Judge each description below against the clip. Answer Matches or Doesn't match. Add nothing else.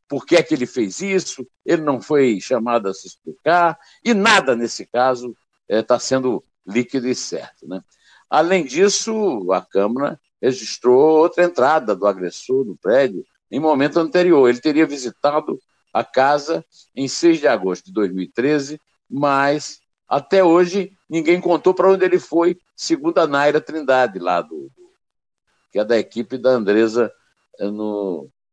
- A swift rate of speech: Doesn't match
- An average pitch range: Doesn't match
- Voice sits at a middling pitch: Matches